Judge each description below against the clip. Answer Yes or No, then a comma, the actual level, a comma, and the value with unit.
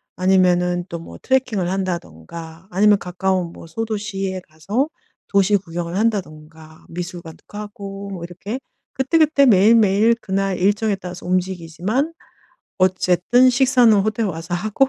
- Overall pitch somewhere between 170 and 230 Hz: Yes, high, 190 Hz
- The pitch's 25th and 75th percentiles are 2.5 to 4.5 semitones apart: Yes, average, 3.5 semitones